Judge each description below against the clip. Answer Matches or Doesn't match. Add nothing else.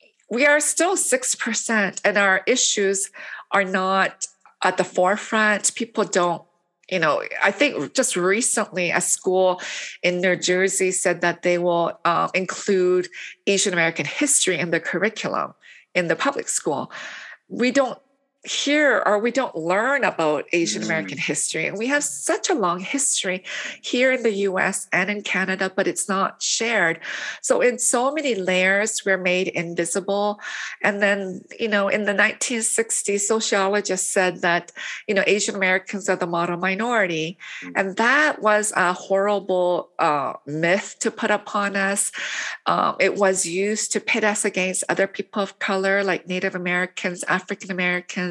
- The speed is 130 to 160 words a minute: Matches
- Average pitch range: Matches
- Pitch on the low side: Doesn't match